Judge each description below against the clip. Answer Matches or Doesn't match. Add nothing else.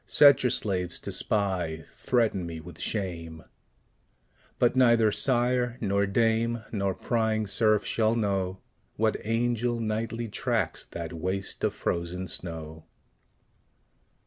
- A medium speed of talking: Doesn't match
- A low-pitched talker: Matches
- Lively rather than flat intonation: Doesn't match